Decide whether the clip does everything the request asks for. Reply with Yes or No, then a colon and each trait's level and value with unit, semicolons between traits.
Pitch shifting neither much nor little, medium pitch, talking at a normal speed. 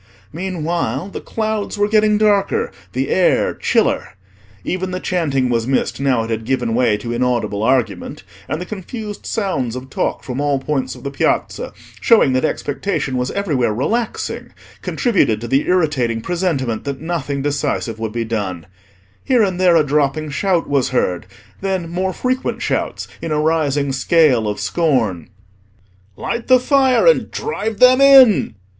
No: wide, 7.4 semitones; medium, 145 Hz; average, 160 wpm